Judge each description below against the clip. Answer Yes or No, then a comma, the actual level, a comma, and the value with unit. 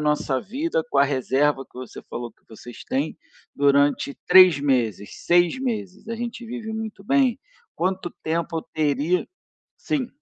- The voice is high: No, medium, 165 Hz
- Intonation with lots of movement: Yes, wide, 7.8 semitones